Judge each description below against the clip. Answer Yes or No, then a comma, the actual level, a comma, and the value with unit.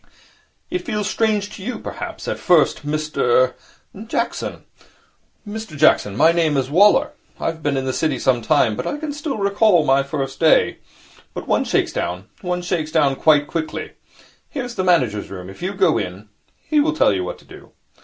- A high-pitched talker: No, medium, 155 Hz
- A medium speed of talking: Yes, average, 195 wpm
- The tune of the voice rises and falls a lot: Yes, wide, 7.0 semitones